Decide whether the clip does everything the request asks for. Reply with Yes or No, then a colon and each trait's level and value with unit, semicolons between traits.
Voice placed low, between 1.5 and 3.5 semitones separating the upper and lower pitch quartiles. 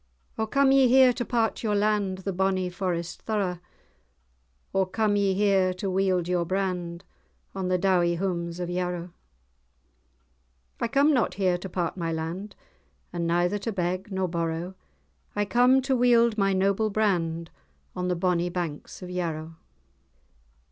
No: medium, 185 Hz; average, 2.9 semitones